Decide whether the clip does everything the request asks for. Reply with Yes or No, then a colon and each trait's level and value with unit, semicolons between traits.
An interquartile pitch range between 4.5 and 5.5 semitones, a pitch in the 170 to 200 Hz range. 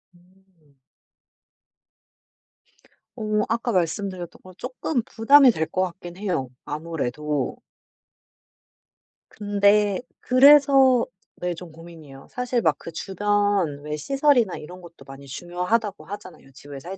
Yes: average, 5.1 semitones; medium, 185 Hz